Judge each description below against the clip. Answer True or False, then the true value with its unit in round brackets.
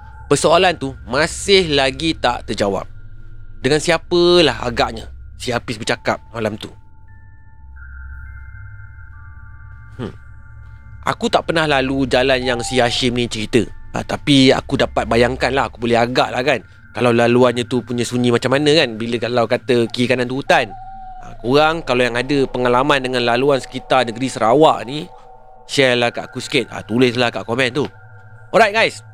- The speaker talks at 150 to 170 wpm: True (155 wpm)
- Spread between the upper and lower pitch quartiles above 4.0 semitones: False (3.5 semitones)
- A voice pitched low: True (120 Hz)